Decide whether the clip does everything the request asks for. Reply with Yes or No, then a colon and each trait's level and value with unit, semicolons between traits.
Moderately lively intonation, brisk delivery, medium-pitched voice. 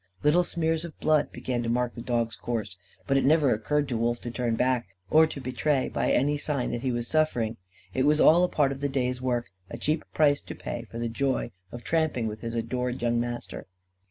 No: average, 3.8 semitones; fast, 225 wpm; low, 125 Hz